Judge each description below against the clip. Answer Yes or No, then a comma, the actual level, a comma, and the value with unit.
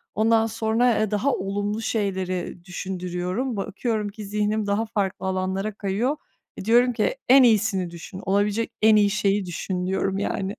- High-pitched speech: Yes, high, 205 Hz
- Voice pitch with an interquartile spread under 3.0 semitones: Yes, narrow, 2.5 semitones